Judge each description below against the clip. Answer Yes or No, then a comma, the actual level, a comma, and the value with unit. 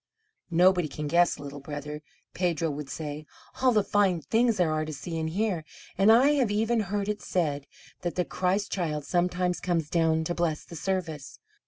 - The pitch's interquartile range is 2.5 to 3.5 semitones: No, average, 4.0 semitones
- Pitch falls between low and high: Yes, medium, 175 Hz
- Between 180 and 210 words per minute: Yes, average, 185 wpm